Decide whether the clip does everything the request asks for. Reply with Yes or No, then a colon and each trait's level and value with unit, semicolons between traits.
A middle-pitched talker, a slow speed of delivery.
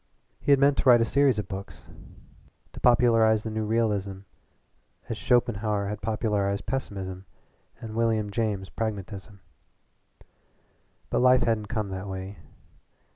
No: low, 110 Hz; slow, 130 wpm